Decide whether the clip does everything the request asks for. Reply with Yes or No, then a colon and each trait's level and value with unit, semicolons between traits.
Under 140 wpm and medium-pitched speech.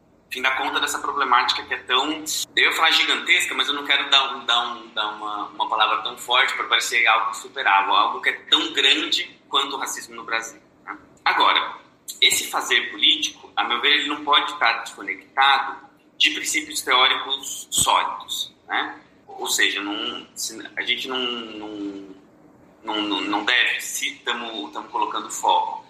No: average, 165 wpm; medium, 145 Hz